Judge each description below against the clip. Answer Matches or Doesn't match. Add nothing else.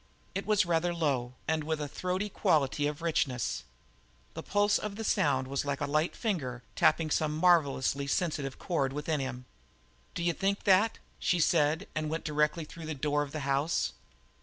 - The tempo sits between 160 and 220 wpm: Matches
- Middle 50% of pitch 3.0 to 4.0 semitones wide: Matches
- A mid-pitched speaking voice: Matches